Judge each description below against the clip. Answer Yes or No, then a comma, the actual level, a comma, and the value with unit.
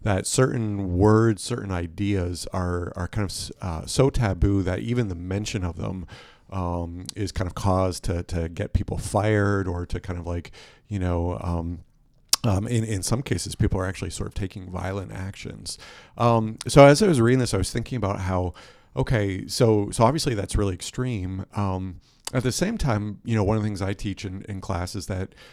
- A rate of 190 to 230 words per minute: Yes, average, 200 wpm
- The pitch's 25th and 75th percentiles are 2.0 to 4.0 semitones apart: Yes, average, 3.6 semitones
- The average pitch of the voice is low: Yes, low, 100 Hz